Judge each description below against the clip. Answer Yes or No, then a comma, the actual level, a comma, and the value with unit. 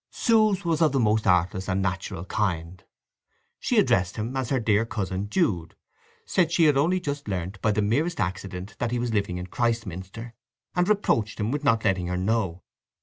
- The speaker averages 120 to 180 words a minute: No, average, 190 wpm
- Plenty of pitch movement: Yes, wide, 6.7 semitones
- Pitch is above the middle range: No, low, 110 Hz